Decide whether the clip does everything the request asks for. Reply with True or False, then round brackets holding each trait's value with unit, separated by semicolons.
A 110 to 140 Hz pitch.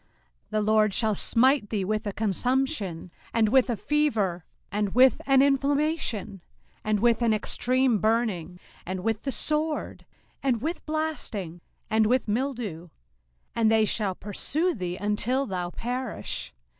False (225 Hz)